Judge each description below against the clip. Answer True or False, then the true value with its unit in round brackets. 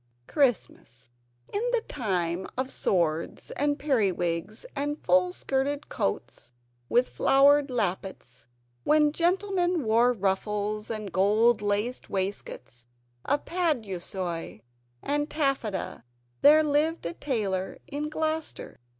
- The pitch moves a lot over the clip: True (7.5 semitones)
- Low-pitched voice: False (230 Hz)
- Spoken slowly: True (105 wpm)